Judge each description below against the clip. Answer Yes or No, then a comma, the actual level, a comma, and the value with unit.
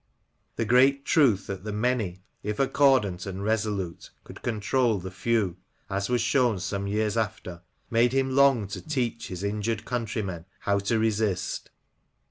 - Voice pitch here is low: Yes, low, 110 Hz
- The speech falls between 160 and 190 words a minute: No, average, 150 wpm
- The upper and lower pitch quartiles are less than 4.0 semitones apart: Yes, average, 3.6 semitones